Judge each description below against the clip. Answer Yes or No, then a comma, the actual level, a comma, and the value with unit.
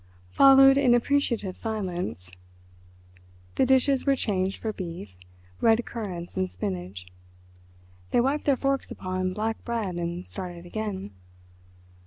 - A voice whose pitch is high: Yes, high, 205 Hz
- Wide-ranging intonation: Yes, wide, 6.2 semitones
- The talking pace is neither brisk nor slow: No, slow, 120 wpm